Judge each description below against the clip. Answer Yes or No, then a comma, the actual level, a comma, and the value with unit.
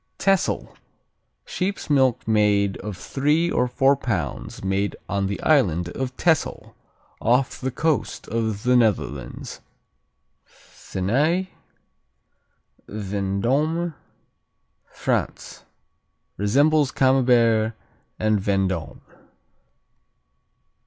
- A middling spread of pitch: No, wide, 5.8 semitones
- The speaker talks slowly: Yes, slow, 80 wpm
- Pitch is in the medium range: No, low, 115 Hz